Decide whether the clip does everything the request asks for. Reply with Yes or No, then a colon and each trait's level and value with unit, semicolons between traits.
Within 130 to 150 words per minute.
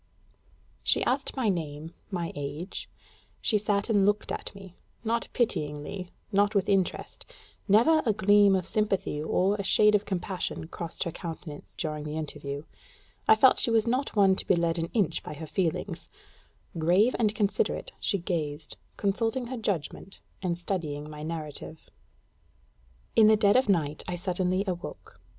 No: average, 160 wpm